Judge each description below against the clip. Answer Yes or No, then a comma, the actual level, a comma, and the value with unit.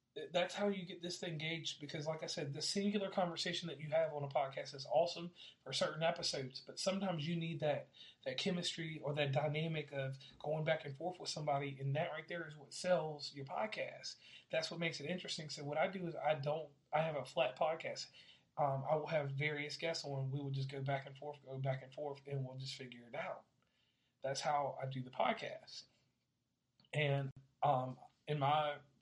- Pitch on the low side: No, medium, 150 Hz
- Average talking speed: No, fast, 210 wpm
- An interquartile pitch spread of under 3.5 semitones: Yes, average, 3.0 semitones